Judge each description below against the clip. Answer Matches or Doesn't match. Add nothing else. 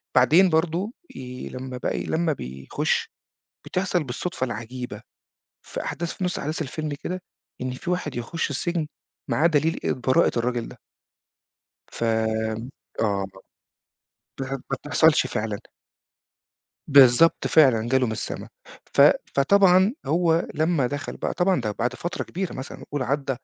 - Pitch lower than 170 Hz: Matches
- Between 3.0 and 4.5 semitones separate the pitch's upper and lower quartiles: Doesn't match